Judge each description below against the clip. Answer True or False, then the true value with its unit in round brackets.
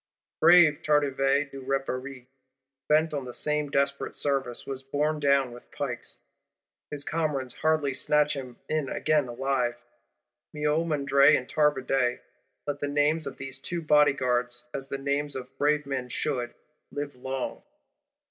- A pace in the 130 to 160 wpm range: True (140 wpm)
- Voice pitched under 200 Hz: True (140 Hz)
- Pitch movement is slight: True (2.1 semitones)